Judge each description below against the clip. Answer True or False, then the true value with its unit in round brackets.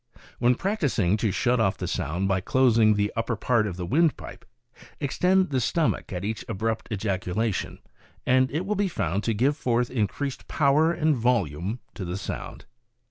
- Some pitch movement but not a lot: False (5.8 semitones)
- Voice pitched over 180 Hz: False (115 Hz)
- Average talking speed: True (170 wpm)